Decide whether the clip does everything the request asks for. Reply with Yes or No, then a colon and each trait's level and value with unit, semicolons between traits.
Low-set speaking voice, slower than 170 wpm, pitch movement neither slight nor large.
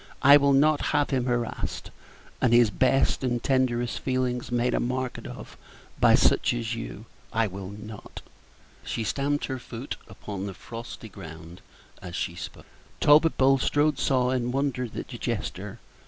Yes: low, 125 Hz; average, 155 wpm; average, 3.4 semitones